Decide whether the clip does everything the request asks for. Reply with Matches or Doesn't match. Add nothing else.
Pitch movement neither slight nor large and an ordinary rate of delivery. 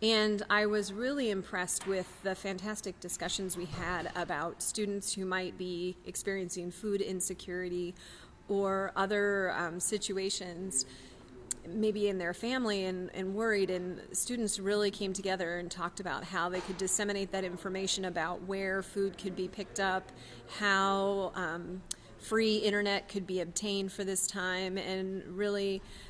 Doesn't match